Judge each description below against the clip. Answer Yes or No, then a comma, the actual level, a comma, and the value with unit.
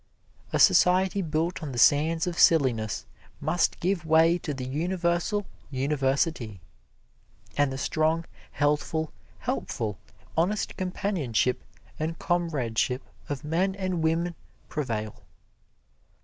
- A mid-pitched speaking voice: Yes, medium, 160 Hz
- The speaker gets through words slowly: Yes, slow, 105 wpm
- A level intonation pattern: No, average, 4.4 semitones